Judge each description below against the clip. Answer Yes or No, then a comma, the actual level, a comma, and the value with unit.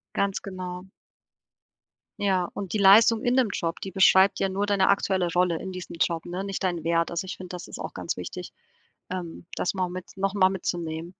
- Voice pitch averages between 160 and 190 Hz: Yes, medium, 185 Hz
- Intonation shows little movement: Yes, narrow, 1.9 semitones